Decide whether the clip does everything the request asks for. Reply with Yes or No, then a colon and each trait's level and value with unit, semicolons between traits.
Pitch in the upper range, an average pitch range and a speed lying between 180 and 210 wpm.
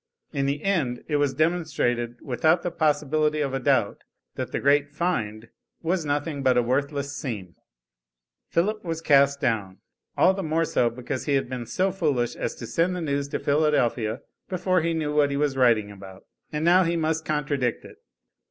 No: medium, 145 Hz; average, 4.3 semitones; average, 185 wpm